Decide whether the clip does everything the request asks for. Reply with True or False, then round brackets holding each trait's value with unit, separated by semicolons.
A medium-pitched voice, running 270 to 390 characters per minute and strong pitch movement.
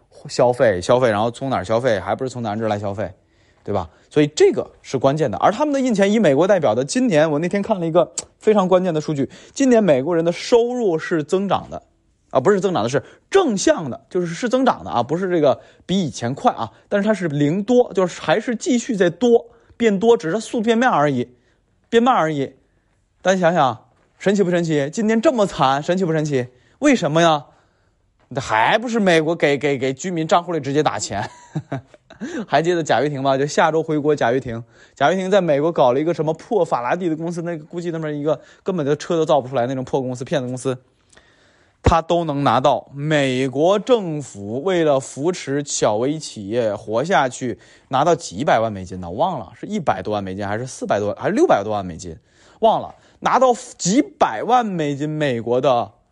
True (155 Hz; 305 characters per minute; 7.3 semitones)